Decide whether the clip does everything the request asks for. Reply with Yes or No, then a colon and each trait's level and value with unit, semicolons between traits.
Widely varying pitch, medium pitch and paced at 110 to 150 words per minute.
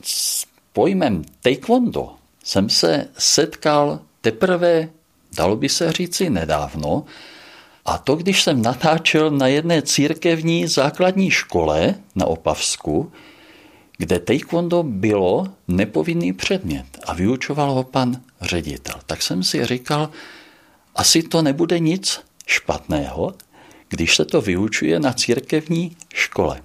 Yes: wide, 5.8 semitones; medium, 145 Hz; slow, 115 wpm